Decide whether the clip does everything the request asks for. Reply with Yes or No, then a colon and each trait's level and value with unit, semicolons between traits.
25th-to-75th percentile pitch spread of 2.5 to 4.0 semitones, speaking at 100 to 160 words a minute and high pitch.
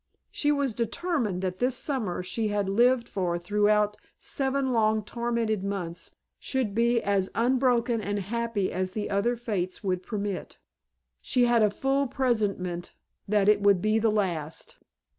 Yes: average, 3.5 semitones; average, 150 wpm; high, 215 Hz